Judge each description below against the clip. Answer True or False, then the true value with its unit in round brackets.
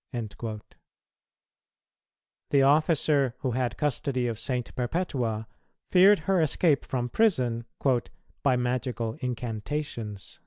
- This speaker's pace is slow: True (95 wpm)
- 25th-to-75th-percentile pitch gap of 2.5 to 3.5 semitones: False (4.2 semitones)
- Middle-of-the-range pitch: False (125 Hz)